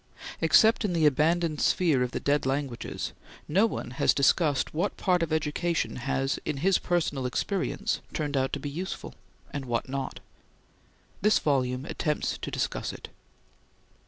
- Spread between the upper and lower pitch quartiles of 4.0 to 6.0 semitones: Yes, average, 4.4 semitones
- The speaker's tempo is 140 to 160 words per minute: Yes, average, 155 wpm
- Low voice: No, medium, 150 Hz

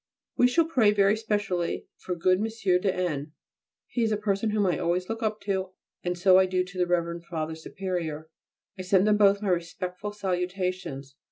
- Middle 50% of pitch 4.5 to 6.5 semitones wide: No, average, 2.8 semitones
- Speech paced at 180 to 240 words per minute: Yes, average, 190 wpm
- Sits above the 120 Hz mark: Yes, medium, 185 Hz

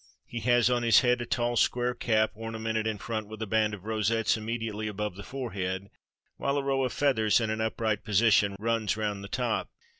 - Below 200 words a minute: No, fast, 205 wpm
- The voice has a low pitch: Yes, low, 110 Hz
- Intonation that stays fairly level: Yes, narrow, 2.0 semitones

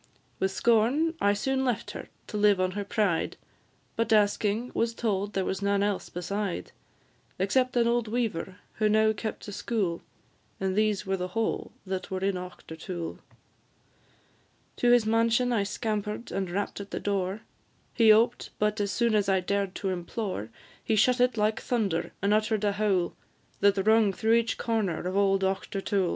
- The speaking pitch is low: No, high, 205 Hz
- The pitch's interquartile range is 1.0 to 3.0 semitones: Yes, narrow, 2.6 semitones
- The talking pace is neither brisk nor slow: Yes, average, 170 wpm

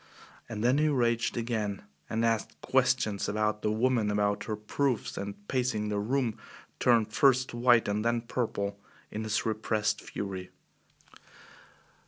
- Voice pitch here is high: No, low, 110 Hz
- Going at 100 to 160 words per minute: Yes, average, 140 wpm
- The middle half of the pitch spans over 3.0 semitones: No, narrow, 2.4 semitones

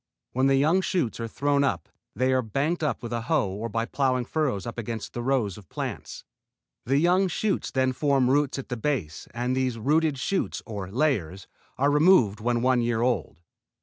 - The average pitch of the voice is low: Yes, low, 130 Hz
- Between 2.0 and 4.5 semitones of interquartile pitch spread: Yes, average, 3.9 semitones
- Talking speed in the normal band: Yes, average, 195 wpm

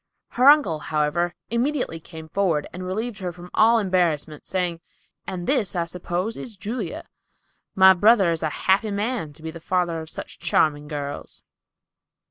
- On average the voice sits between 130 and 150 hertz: No, medium, 180 Hz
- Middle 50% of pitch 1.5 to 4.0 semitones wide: No, average, 4.5 semitones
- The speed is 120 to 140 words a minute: No, average, 160 wpm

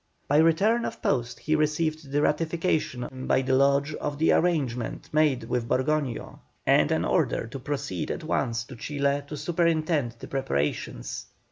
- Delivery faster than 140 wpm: Yes, average, 155 wpm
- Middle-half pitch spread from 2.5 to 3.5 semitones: Yes, average, 3.2 semitones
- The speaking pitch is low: No, medium, 145 Hz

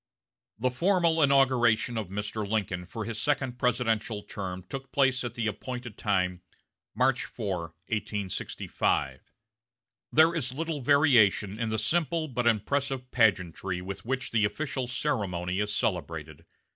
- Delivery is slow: Yes, slow, 130 wpm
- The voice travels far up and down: No, average, 4.6 semitones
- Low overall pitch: Yes, low, 115 Hz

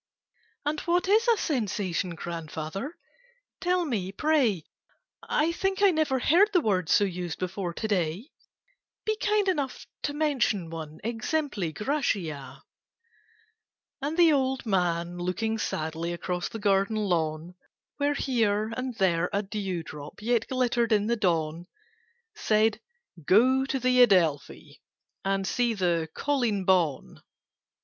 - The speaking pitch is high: Yes, high, 210 Hz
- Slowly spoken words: Yes, slow, 130 wpm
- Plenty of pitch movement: Yes, wide, 7.5 semitones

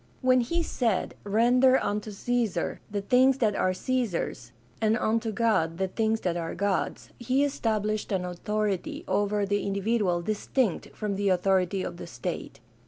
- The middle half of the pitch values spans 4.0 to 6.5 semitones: No, average, 3.6 semitones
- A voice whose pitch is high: Yes, high, 210 Hz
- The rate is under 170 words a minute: Yes, average, 155 wpm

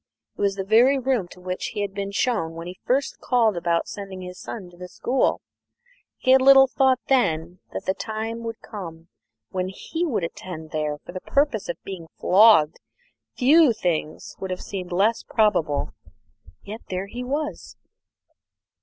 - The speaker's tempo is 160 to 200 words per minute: Yes, average, 170 wpm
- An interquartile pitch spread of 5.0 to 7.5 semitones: Yes, wide, 5.4 semitones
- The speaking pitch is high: Yes, high, 200 Hz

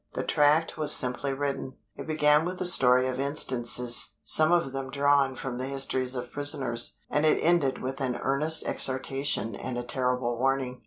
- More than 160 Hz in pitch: No, low, 135 Hz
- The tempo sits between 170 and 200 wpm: Yes, average, 175 wpm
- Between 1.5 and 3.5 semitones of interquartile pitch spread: Yes, narrow, 2.4 semitones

